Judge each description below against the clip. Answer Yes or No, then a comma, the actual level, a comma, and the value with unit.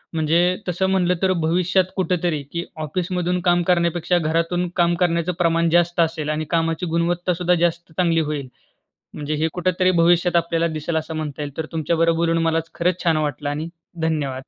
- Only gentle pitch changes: Yes, narrow, 1.6 semitones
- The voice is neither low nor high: Yes, medium, 170 Hz